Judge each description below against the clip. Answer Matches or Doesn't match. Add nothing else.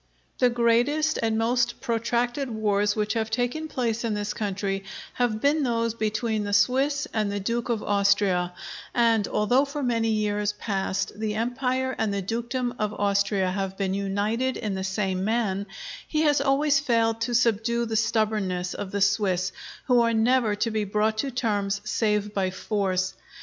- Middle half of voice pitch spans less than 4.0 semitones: Matches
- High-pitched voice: Matches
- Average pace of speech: Matches